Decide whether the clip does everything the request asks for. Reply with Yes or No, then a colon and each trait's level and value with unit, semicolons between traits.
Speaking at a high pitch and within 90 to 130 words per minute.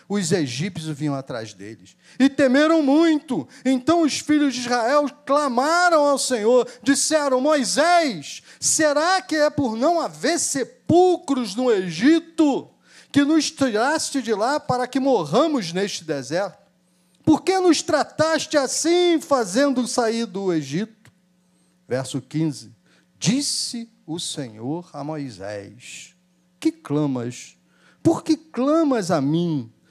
Yes: very high, 250 Hz; slow, 120 wpm